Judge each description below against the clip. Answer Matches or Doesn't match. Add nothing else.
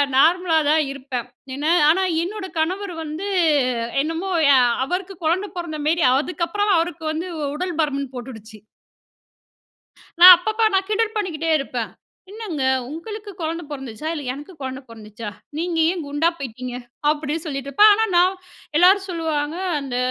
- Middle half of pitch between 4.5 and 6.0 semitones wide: Matches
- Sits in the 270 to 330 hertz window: Matches